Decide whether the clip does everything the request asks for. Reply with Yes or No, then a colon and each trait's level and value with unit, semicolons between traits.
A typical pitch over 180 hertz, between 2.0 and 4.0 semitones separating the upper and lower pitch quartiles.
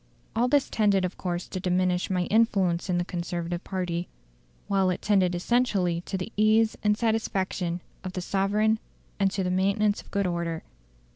Yes: high, 190 Hz; average, 2.8 semitones